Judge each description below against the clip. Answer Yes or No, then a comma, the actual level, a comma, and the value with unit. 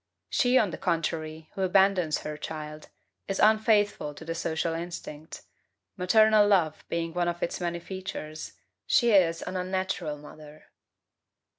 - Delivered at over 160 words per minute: No, average, 140 wpm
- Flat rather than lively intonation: No, average, 3.6 semitones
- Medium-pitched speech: Yes, medium, 175 Hz